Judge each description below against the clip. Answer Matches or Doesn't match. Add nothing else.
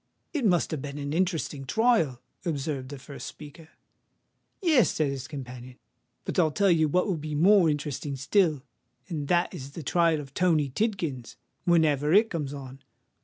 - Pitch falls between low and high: Matches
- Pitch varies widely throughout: Doesn't match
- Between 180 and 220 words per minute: Doesn't match